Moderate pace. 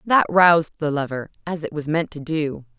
No: fast, 215 wpm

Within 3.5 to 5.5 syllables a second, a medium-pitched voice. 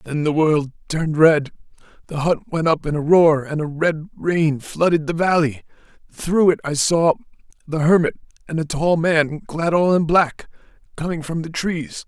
Yes: 4.6 syllables/s; medium, 160 Hz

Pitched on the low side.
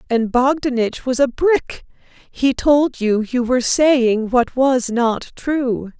No: very high, 250 Hz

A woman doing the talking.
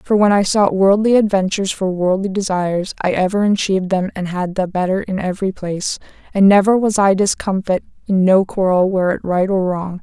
Yes: female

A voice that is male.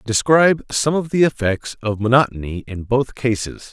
Yes: male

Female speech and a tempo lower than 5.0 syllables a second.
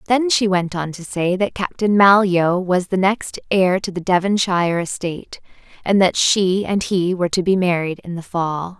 Yes: female; 4.7 syllables/s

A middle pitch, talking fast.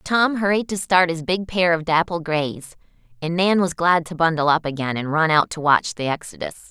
Yes: medium, 165 Hz; fast, 225 wpm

